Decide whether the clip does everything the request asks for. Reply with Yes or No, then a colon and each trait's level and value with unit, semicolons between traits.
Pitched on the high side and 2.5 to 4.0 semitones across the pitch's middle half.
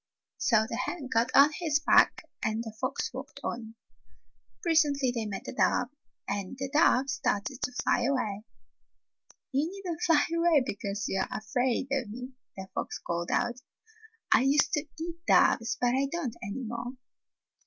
No: very high, 255 Hz; average, 4.6 semitones